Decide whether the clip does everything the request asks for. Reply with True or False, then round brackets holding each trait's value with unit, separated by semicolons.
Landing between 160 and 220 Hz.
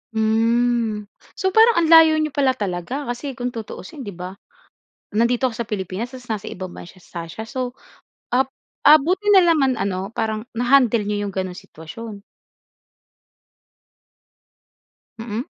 False (230 Hz)